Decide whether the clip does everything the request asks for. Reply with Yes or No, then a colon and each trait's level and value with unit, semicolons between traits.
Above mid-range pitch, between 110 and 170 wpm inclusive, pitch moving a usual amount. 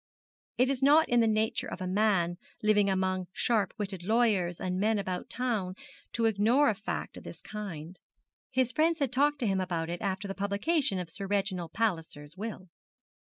No: high, 200 Hz; average, 185 wpm; average, 3.7 semitones